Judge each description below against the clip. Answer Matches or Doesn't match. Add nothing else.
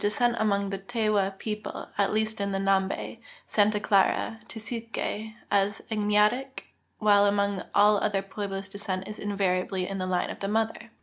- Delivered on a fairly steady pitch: Matches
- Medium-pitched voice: Doesn't match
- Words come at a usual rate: Matches